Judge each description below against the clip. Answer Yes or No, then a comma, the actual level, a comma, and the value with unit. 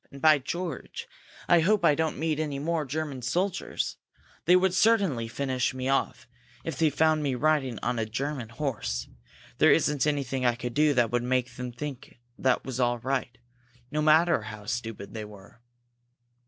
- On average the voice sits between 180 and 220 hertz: No, low, 135 Hz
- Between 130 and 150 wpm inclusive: No, average, 175 wpm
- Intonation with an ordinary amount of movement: Yes, average, 4.3 semitones